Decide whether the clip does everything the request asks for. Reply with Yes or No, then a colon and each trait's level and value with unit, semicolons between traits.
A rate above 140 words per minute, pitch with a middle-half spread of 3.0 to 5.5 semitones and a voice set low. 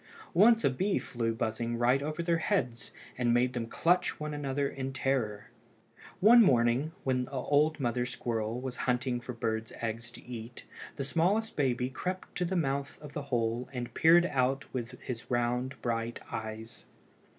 Yes: average, 175 wpm; average, 3.8 semitones; low, 125 Hz